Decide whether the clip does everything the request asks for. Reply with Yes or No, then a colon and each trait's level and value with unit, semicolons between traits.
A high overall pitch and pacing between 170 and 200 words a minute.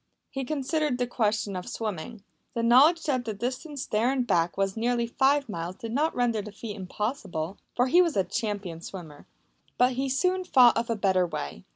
Yes: high, 235 Hz; average, 195 wpm